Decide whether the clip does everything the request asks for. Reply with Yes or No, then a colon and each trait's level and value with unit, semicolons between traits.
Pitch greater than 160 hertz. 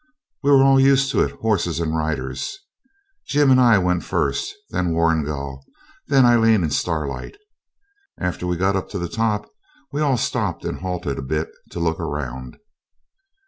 No: very low, 90 Hz